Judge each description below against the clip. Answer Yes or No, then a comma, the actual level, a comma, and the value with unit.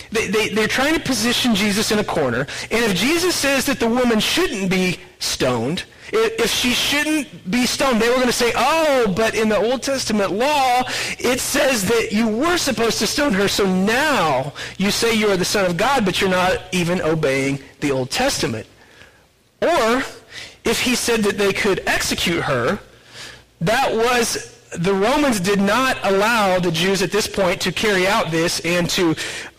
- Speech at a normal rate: Yes, average, 185 wpm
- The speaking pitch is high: Yes, high, 220 Hz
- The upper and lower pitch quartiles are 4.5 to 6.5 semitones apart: Yes, average, 4.9 semitones